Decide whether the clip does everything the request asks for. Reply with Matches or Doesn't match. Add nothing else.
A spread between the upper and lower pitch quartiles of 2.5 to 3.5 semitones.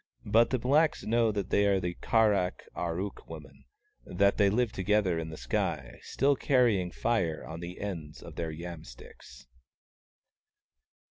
Doesn't match